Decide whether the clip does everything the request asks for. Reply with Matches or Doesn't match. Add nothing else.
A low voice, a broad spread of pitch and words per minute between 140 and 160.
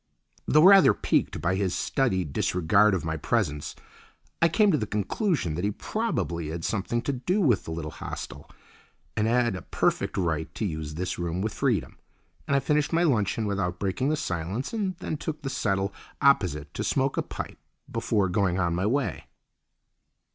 Doesn't match